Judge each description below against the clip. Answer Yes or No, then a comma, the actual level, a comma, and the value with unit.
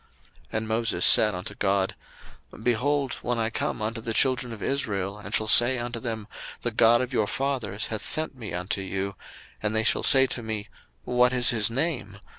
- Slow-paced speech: No, average, 195 wpm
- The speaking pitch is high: No, low, 115 Hz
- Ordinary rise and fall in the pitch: Yes, average, 3.1 semitones